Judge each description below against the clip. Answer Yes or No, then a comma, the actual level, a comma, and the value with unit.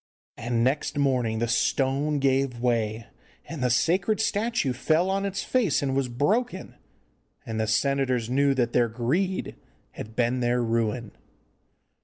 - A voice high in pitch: No, low, 130 Hz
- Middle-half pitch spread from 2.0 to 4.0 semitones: No, average, 4.6 semitones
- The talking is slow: No, average, 145 wpm